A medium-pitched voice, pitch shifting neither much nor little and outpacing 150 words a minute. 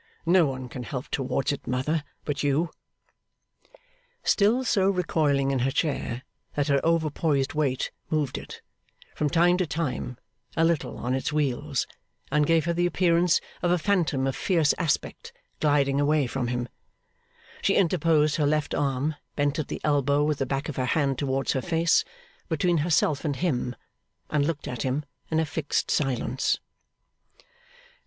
Yes: medium, 150 Hz; average, 3.3 semitones; average, 160 wpm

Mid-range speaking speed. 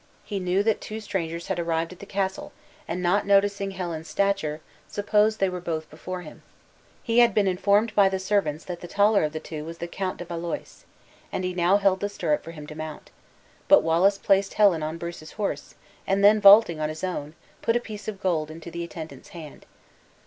No: fast, 210 wpm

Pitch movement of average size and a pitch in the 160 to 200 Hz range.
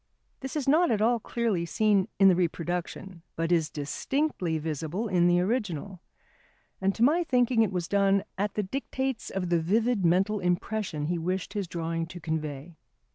Yes: average, 4.6 semitones; high, 190 Hz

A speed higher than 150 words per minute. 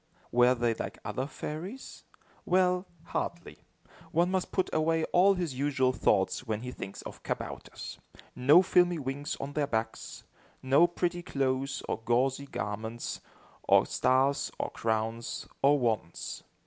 No: slow, 135 wpm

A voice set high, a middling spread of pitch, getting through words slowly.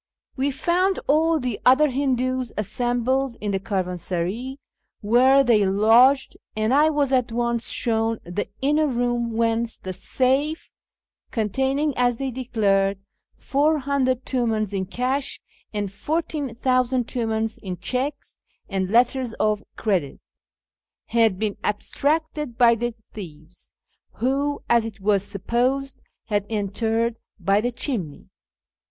Yes: high, 235 Hz; average, 4.1 semitones; slow, 120 wpm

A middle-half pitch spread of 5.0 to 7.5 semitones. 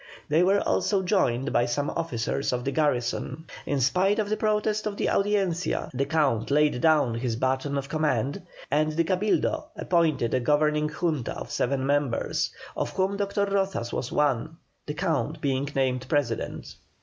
Yes: wide, 5.6 semitones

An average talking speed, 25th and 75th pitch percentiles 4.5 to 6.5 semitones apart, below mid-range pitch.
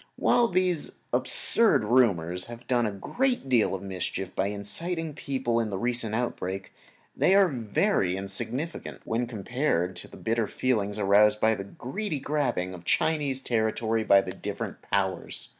Yes: average, 160 wpm; wide, 5.6 semitones; low, 115 Hz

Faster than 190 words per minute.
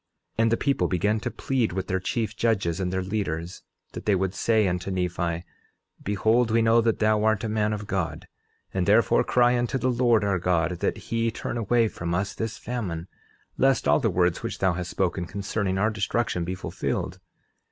Yes: average, 200 wpm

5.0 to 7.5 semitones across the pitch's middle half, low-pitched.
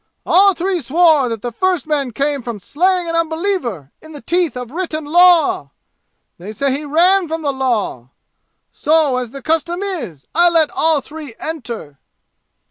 No: wide, 5.5 semitones; very high, 305 Hz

